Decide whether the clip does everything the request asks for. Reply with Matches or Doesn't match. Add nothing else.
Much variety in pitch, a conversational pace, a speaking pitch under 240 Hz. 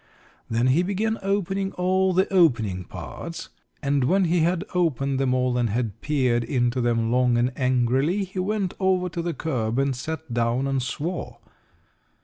Matches